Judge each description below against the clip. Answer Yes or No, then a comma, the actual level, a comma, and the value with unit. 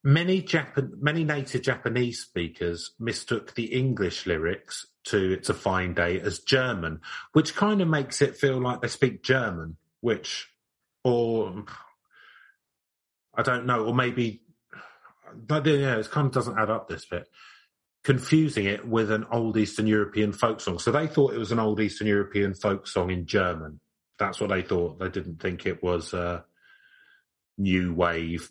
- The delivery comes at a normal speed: Yes, average, 165 wpm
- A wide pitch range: Yes, wide, 6.2 semitones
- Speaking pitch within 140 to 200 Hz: No, low, 115 Hz